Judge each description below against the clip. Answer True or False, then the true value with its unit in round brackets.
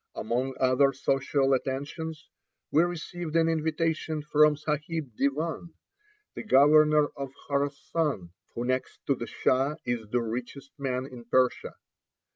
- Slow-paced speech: True (125 wpm)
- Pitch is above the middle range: False (140 Hz)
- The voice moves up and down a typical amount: True (3.2 semitones)